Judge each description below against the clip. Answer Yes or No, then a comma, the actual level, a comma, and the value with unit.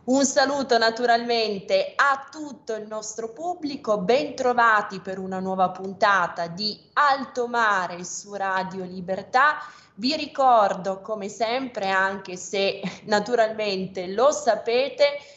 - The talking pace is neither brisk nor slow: No, slow, 110 wpm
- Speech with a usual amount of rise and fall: No, wide, 5.9 semitones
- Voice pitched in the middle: No, high, 225 Hz